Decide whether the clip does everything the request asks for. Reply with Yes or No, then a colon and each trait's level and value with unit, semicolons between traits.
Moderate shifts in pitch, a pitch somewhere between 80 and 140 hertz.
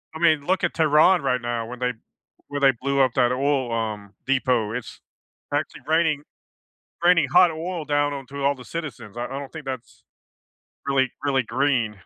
Yes: average, 3.6 semitones; low, 135 Hz